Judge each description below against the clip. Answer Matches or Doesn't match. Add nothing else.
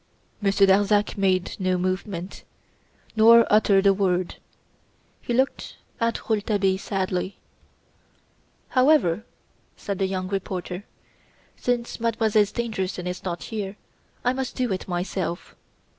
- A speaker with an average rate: Doesn't match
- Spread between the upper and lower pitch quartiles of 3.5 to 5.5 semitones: Doesn't match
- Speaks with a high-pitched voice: Matches